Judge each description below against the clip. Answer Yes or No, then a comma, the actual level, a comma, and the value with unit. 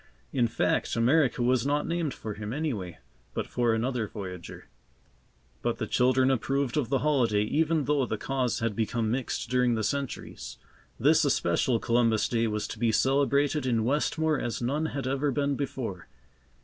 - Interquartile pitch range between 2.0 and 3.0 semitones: No, average, 3.7 semitones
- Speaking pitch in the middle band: No, low, 125 Hz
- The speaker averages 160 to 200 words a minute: Yes, average, 165 wpm